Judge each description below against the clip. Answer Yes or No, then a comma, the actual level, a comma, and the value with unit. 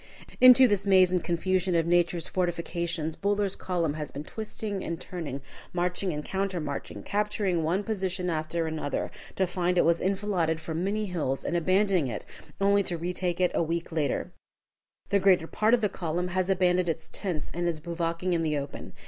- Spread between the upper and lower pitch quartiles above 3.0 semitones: No, average, 2.7 semitones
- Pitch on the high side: No, medium, 175 Hz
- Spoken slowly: No, average, 180 wpm